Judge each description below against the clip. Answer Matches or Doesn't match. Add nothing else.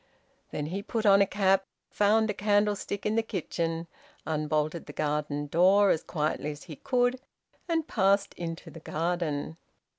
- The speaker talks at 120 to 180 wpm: Matches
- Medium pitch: Matches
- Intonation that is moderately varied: Matches